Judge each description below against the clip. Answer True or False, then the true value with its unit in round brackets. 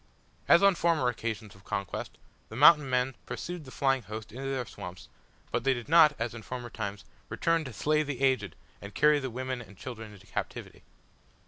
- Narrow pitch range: False (4.8 semitones)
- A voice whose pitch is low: True (125 Hz)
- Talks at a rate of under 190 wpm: False (195 wpm)